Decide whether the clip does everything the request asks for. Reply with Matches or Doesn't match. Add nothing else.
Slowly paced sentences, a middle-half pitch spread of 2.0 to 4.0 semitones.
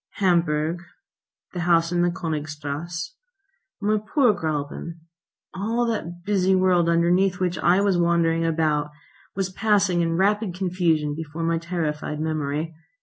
Matches